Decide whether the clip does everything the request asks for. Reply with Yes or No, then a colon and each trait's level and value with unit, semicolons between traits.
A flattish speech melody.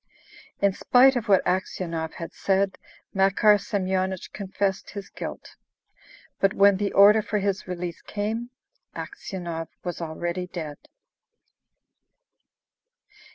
Yes: narrow, 2.2 semitones